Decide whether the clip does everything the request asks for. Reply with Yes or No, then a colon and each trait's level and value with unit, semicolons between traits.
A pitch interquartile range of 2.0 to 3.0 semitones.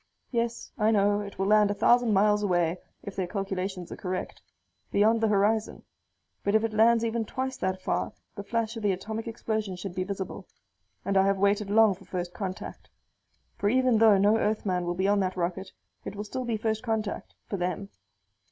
Yes: narrow, 2.5 semitones